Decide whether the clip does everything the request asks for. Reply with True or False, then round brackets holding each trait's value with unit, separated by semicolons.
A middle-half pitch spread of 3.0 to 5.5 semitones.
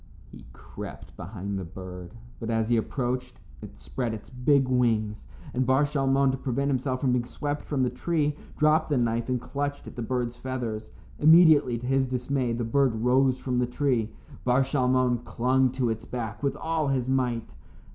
False (2.5 semitones)